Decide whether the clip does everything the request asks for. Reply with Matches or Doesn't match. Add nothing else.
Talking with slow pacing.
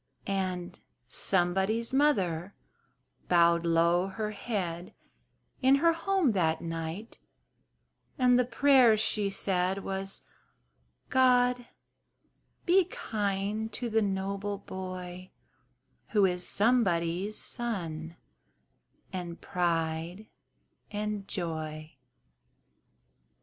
Matches